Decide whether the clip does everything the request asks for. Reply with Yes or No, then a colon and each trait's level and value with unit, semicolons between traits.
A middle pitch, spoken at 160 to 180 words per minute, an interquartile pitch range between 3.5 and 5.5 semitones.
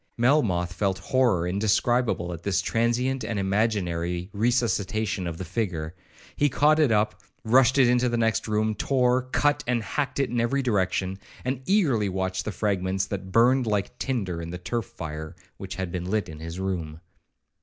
No: low, 105 Hz; average, 170 wpm; average, 5.0 semitones